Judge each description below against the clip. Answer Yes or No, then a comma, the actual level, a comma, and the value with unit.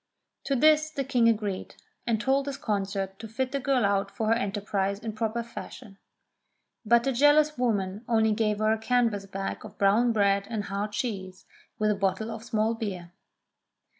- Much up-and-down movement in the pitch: No, average, 3.2 semitones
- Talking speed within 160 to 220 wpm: Yes, average, 180 wpm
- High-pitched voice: Yes, high, 220 Hz